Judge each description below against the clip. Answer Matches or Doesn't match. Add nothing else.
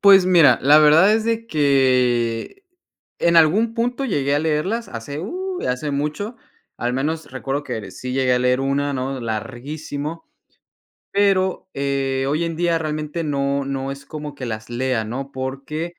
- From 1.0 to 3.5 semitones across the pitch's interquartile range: Doesn't match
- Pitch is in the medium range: Matches